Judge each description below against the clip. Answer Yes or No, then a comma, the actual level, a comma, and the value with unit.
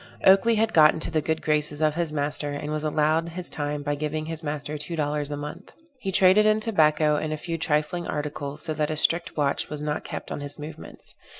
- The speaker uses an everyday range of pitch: No, narrow, 2.0 semitones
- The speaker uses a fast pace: Yes, fast, 225 wpm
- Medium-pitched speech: Yes, medium, 155 Hz